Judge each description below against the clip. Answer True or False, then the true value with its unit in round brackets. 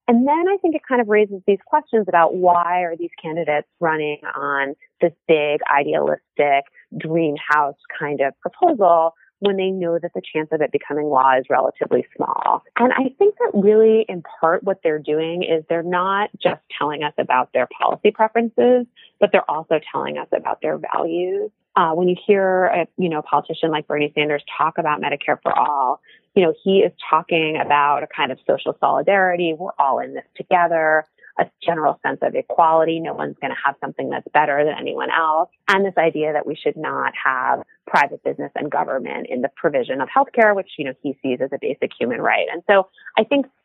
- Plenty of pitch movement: True (5.9 semitones)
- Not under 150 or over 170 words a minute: False (200 wpm)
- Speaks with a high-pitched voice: False (175 Hz)